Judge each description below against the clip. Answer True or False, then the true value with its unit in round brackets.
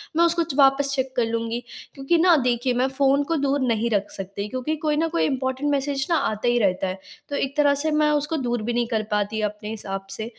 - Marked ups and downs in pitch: False (4.3 semitones)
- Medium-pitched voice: False (255 Hz)